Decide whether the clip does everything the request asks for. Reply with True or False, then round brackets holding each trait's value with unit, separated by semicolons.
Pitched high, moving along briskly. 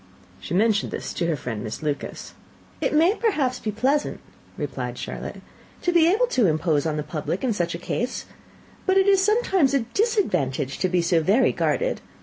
False (225 Hz; 185 wpm)